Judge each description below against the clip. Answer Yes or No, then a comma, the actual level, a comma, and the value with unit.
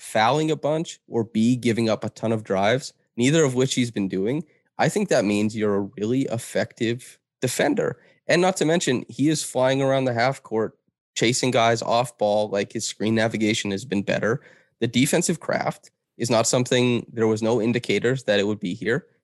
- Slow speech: No, average, 195 wpm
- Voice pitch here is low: Yes, low, 115 Hz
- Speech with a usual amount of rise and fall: Yes, average, 3.2 semitones